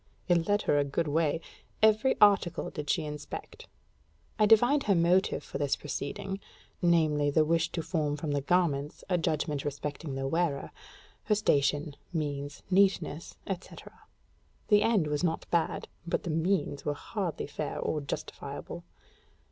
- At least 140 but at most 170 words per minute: Yes, average, 150 wpm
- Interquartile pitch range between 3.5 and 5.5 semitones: Yes, average, 4.0 semitones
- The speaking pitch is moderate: Yes, medium, 160 Hz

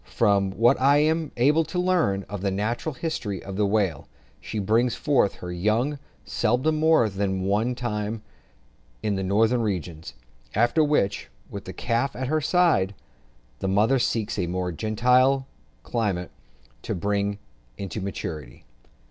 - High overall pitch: No, low, 110 Hz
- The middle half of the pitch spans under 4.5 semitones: No, average, 5.0 semitones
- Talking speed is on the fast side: No, average, 155 wpm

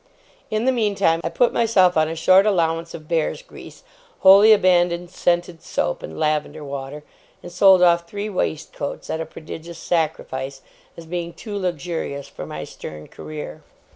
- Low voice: No, medium, 170 Hz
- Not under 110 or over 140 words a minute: No, average, 160 wpm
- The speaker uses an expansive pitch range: No, average, 3.3 semitones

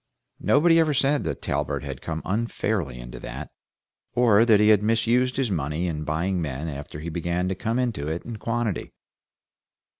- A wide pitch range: Yes, wide, 6.7 semitones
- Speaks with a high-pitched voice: No, low, 100 Hz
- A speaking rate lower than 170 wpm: No, average, 175 wpm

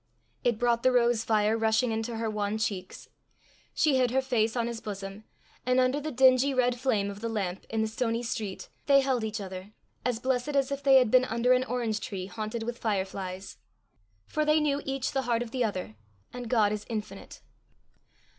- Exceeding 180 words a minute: Yes, average, 200 wpm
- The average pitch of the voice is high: Yes, high, 230 Hz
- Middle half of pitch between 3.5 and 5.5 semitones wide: No, average, 3.1 semitones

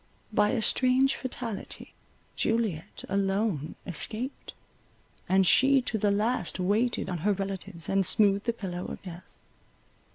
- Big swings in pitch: No, average, 3.6 semitones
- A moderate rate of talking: No, slow, 130 wpm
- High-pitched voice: Yes, high, 200 Hz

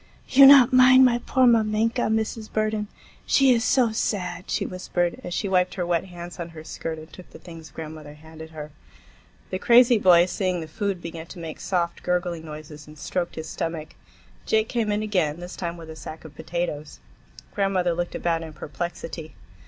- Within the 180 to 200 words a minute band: Yes, average, 190 wpm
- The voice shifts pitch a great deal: No, average, 4.9 semitones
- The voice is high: No, medium, 175 Hz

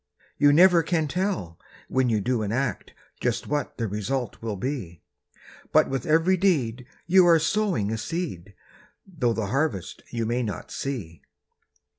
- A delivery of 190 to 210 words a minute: No, average, 155 wpm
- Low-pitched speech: Yes, low, 130 Hz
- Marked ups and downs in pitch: Yes, wide, 7.1 semitones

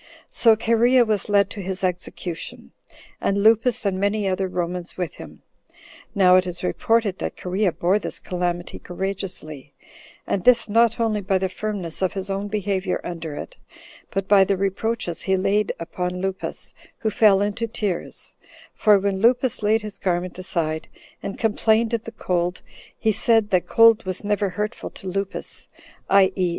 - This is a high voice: Yes, high, 195 Hz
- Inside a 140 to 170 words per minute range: Yes, average, 165 wpm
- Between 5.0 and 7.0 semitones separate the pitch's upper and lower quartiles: No, average, 2.8 semitones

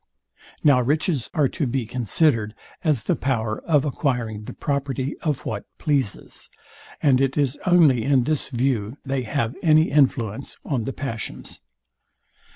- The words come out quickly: No, average, 145 wpm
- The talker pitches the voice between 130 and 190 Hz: Yes, low, 135 Hz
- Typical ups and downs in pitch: Yes, average, 3.8 semitones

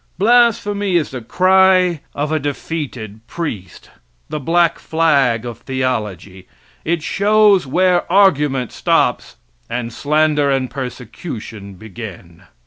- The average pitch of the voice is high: No, medium, 145 Hz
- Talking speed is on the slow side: Yes, slow, 110 wpm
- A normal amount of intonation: No, wide, 6.9 semitones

